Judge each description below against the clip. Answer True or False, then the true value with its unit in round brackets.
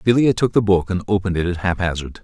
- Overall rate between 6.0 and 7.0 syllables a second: True (6.6 syllables/s)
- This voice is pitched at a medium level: False (95 Hz)